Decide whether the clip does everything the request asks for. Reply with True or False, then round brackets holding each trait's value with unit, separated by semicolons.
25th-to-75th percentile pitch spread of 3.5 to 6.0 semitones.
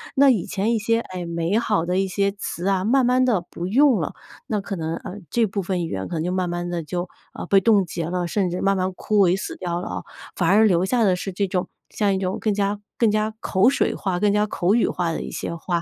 False (3.0 semitones)